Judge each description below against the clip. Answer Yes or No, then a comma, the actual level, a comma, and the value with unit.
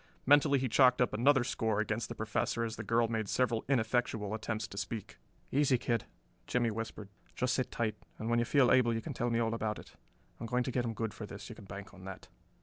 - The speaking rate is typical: No, fast, 240 wpm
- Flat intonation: Yes, narrow, 2.3 semitones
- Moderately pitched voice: No, low, 115 Hz